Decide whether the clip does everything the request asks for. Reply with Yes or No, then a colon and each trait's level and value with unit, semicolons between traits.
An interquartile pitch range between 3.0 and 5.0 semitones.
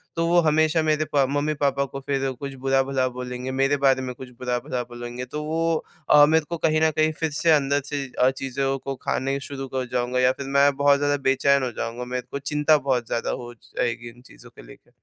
No: narrow, 2.6 semitones